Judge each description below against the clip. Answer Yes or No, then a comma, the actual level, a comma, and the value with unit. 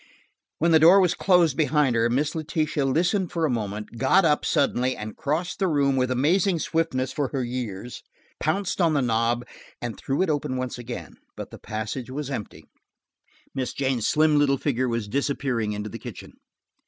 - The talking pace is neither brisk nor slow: Yes, average, 180 wpm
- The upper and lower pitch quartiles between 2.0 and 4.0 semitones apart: No, average, 4.5 semitones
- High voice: No, low, 135 Hz